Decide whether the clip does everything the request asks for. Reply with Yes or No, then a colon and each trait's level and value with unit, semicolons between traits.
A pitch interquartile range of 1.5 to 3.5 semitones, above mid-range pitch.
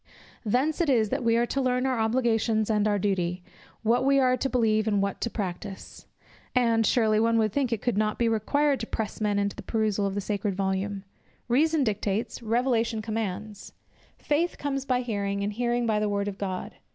Yes: average, 3.2 semitones; high, 220 Hz